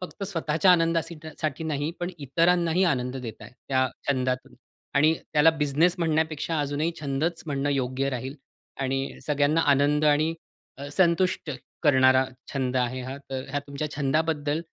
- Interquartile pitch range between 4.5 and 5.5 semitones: No, average, 3.2 semitones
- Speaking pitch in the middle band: Yes, medium, 145 Hz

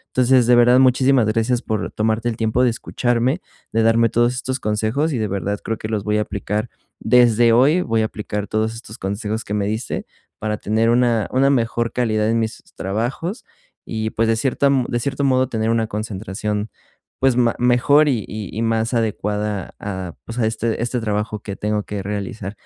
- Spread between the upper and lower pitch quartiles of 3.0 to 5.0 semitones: No, narrow, 2.5 semitones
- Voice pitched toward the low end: Yes, low, 115 Hz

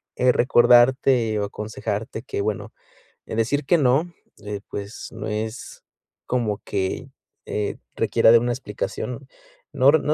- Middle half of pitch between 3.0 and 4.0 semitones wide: Yes, average, 3.4 semitones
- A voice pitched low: Yes, low, 115 Hz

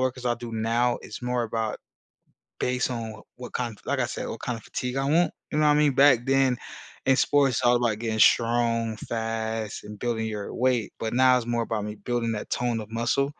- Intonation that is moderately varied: No, narrow, 2.1 semitones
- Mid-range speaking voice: No, low, 120 Hz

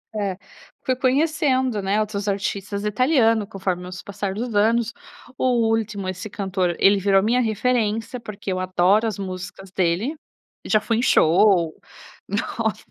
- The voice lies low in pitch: No, high, 205 Hz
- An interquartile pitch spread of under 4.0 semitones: Yes, average, 3.0 semitones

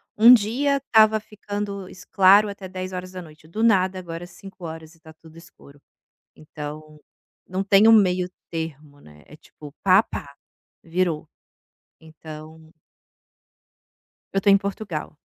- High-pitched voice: No, medium, 180 Hz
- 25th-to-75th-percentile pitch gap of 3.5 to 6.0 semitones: Yes, average, 4.1 semitones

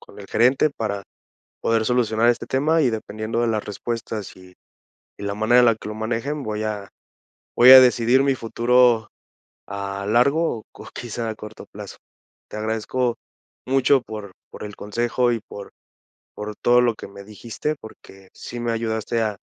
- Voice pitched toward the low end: Yes, low, 115 Hz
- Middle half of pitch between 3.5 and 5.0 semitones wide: No, narrow, 2.4 semitones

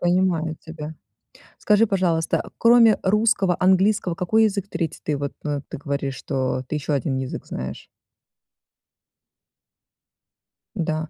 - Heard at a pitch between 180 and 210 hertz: No, medium, 165 Hz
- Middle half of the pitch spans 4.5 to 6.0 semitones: Yes, average, 5.0 semitones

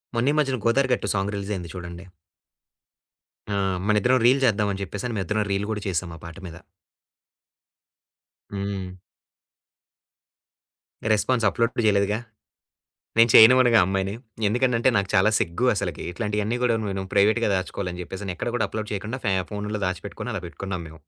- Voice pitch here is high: No, low, 105 Hz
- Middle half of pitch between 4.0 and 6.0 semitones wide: No, average, 3.3 semitones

